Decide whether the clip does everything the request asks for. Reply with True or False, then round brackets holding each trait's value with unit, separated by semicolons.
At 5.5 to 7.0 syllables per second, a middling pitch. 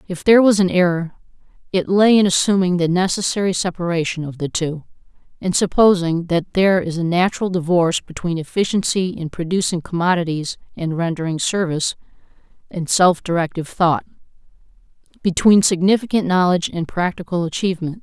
True (5.8 syllables/s; 175 Hz)